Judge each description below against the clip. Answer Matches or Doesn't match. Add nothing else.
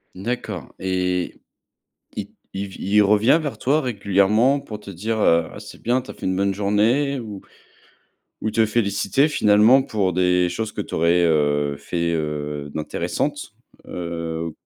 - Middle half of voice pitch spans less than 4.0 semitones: Doesn't match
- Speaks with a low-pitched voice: Matches